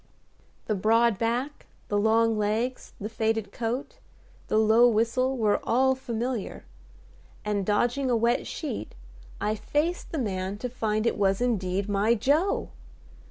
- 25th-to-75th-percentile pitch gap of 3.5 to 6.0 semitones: No, average, 2.9 semitones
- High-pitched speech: Yes, high, 225 Hz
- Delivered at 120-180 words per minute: Yes, average, 140 wpm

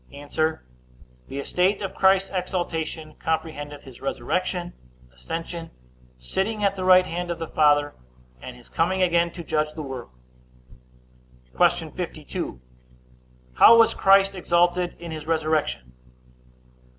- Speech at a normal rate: No, slow, 125 wpm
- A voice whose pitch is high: No, medium, 165 Hz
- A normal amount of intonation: Yes, average, 3.9 semitones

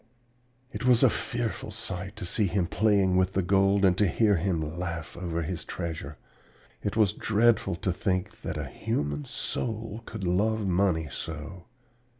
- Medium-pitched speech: No, very low, 95 Hz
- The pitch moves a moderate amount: Yes, average, 3.3 semitones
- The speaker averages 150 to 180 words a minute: Yes, average, 160 wpm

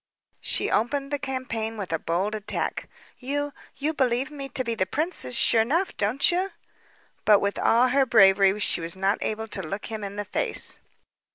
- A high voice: Yes, high, 225 Hz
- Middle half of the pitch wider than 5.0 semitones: Yes, wide, 5.4 semitones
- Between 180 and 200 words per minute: Yes, average, 185 wpm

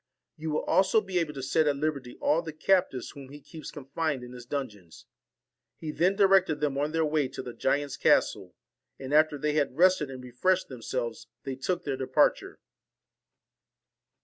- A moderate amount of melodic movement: Yes, average, 3.4 semitones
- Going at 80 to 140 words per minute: No, average, 180 wpm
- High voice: No, medium, 145 Hz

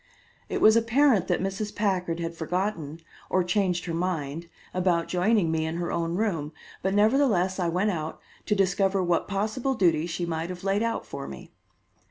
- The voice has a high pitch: No, medium, 180 Hz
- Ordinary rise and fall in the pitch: Yes, average, 3.5 semitones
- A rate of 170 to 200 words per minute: Yes, average, 180 wpm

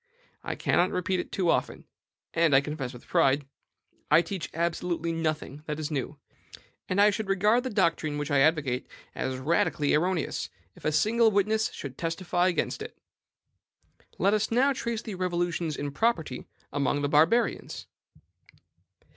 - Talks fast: No, average, 155 wpm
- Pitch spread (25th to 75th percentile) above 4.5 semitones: Yes, average, 4.9 semitones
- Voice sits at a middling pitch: Yes, medium, 165 Hz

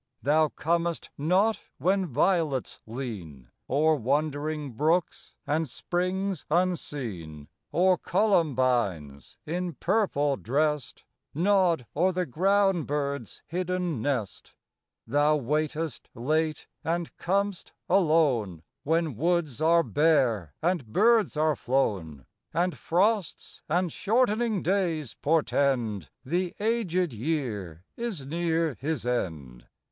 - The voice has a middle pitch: Yes, medium, 155 Hz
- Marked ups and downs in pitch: Yes, wide, 5.7 semitones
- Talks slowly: Yes, slow, 100 wpm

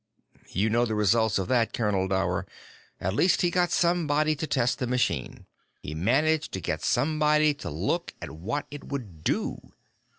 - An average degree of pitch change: No, wide, 7.2 semitones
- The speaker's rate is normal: Yes, average, 170 wpm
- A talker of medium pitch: No, low, 125 Hz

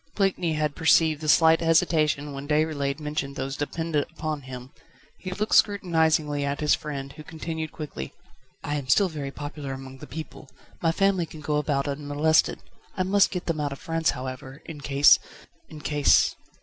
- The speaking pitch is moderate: Yes, medium, 150 Hz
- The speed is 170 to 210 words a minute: Yes, average, 175 wpm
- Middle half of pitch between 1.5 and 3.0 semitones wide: Yes, narrow, 2.4 semitones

